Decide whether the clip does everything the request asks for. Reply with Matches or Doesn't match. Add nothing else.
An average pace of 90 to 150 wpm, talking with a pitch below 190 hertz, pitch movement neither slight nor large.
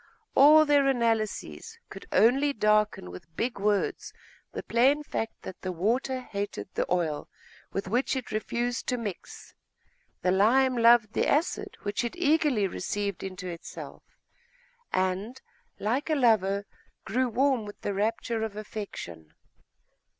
Doesn't match